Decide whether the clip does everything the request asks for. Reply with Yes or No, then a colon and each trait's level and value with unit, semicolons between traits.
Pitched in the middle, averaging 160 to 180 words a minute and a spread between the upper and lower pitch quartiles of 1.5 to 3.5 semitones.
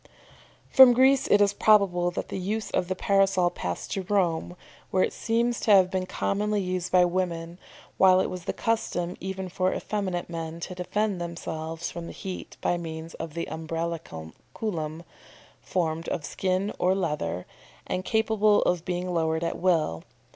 Yes: medium, 180 Hz; average, 170 wpm; average, 2.8 semitones